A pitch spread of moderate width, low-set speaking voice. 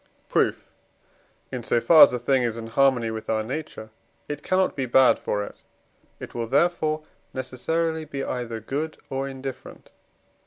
Yes: average, 4.7 semitones; low, 130 Hz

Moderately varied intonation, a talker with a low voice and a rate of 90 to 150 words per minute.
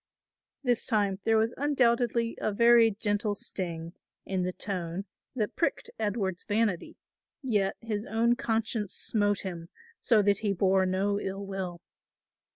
No: average, 3.0 semitones; high, 205 Hz; average, 140 wpm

